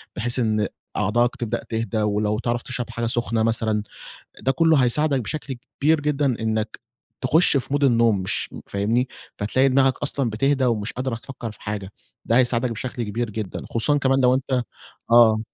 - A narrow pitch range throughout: No, average, 3.2 semitones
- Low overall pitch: Yes, low, 120 Hz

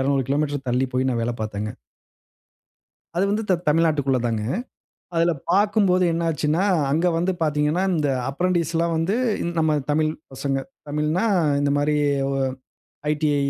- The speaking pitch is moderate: Yes, medium, 150 Hz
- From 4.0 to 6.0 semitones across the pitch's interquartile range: No, average, 3.4 semitones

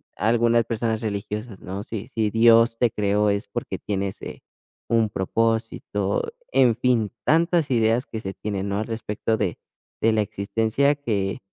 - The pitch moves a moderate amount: No, narrow, 2.3 semitones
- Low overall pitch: Yes, low, 110 Hz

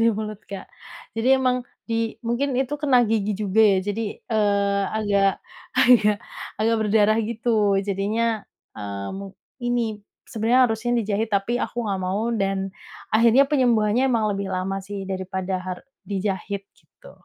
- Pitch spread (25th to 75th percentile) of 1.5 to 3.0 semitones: Yes, average, 2.7 semitones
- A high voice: Yes, high, 215 Hz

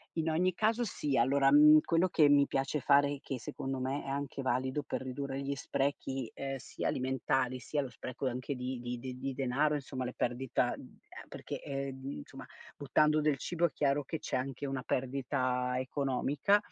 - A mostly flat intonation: Yes, narrow, 2.0 semitones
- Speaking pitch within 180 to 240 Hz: No, low, 135 Hz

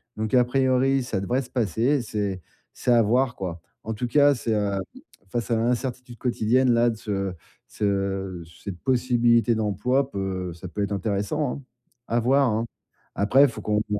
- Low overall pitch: Yes, low, 115 Hz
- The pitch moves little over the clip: No, average, 4.0 semitones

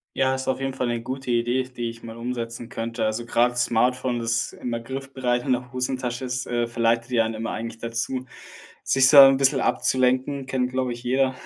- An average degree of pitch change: No, narrow, 1.9 semitones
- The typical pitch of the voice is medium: No, low, 125 Hz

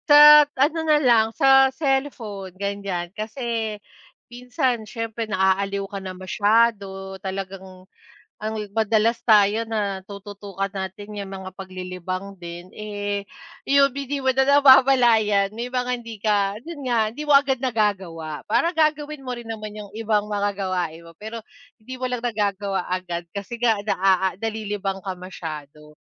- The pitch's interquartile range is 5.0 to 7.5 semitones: No, average, 4.0 semitones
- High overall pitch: Yes, high, 210 Hz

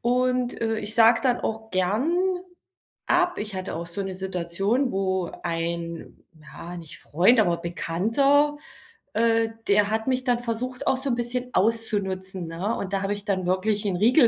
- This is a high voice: Yes, high, 210 Hz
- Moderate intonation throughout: Yes, average, 4.5 semitones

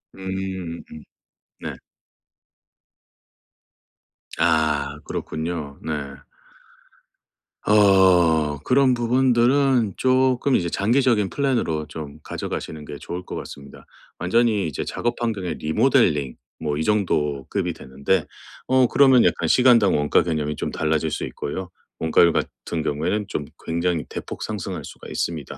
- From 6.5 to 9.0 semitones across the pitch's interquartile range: Yes, wide, 7.2 semitones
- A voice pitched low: Yes, very low, 90 Hz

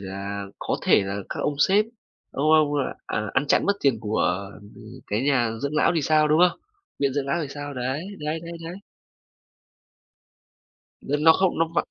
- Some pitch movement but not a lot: No, wide, 5.7 semitones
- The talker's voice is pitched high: No, medium, 145 Hz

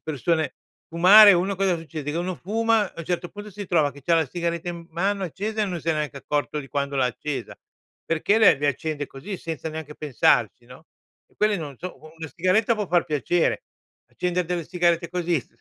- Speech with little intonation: No, average, 3.5 semitones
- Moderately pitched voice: Yes, medium, 170 Hz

